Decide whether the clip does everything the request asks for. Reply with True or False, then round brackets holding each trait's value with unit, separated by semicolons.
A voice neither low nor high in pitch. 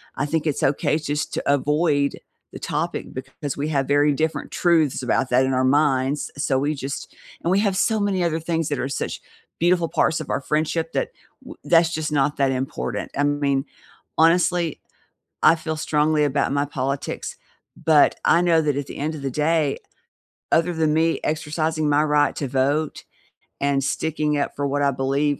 True (150 Hz)